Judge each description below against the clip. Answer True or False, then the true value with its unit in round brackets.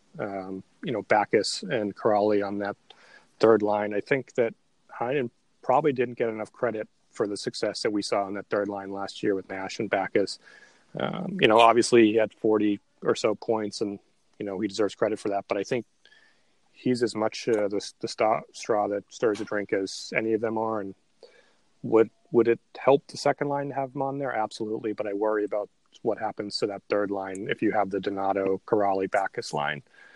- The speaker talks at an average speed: False (210 wpm)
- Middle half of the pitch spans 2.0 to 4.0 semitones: True (2.4 semitones)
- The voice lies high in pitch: False (105 Hz)